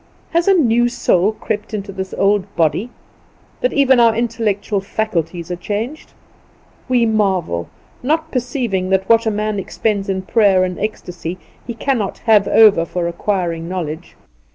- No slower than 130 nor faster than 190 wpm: Yes, average, 150 wpm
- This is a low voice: No, high, 205 Hz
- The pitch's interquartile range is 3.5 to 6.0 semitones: Yes, average, 3.8 semitones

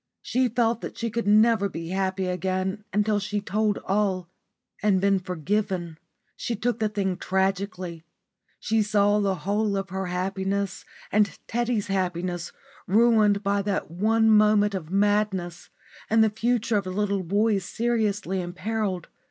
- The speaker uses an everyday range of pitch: No, narrow, 2.3 semitones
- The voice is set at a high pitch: Yes, high, 200 Hz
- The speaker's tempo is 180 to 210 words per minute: No, average, 150 wpm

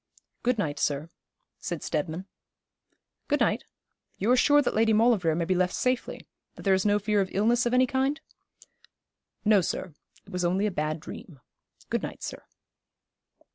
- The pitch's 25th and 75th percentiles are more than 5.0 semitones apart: Yes, wide, 5.6 semitones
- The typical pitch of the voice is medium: No, high, 200 Hz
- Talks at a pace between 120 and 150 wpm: No, average, 170 wpm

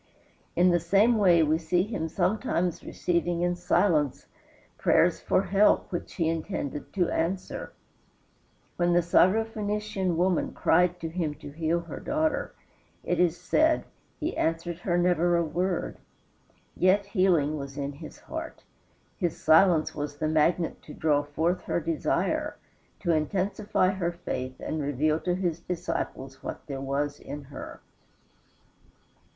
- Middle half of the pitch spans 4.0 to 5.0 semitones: No, average, 3.0 semitones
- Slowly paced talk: No, average, 145 wpm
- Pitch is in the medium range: Yes, medium, 170 Hz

